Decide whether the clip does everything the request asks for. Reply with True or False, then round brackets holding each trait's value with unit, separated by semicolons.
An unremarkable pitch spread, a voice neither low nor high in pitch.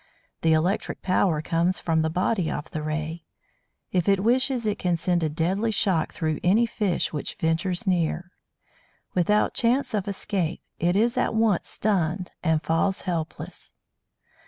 True (4.0 semitones; 180 Hz)